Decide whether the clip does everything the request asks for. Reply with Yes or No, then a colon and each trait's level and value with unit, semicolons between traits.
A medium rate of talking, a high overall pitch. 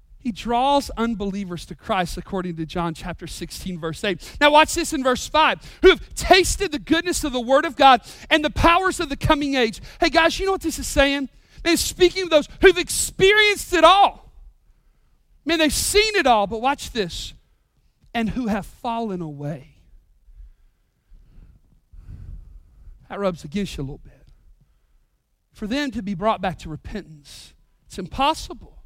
Yes: average, 170 wpm; high, 240 Hz